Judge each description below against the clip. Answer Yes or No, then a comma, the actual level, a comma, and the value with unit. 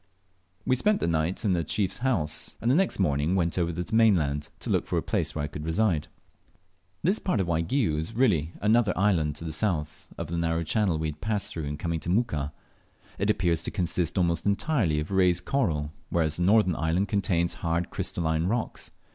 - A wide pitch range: No, average, 4.7 semitones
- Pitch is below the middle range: Yes, very low, 85 Hz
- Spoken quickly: Yes, fast, 210 wpm